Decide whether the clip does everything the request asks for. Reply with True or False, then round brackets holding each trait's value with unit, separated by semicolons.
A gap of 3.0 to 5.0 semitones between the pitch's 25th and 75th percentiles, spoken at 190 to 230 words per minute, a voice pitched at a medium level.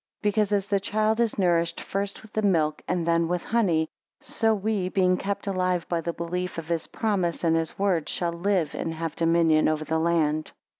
True (3.4 semitones; 195 wpm; 175 Hz)